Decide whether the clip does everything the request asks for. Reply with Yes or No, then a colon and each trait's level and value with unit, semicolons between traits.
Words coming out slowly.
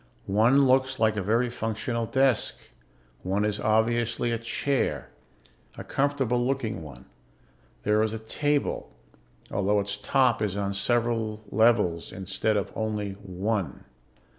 Yes: slow, 130 wpm